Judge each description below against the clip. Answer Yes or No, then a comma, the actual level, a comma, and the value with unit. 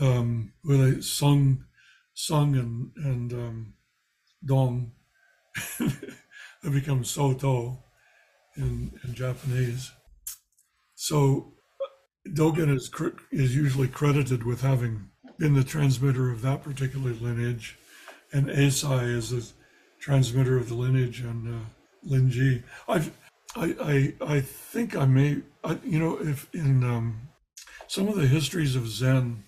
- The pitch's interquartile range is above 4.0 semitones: No, average, 2.7 semitones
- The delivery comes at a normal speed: No, slow, 120 wpm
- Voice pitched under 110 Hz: No, low, 130 Hz